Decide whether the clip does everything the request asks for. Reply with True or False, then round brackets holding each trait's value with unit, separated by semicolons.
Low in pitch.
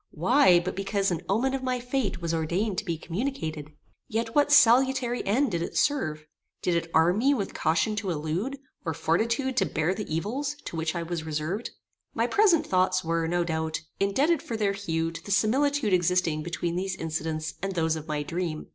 False (185 Hz)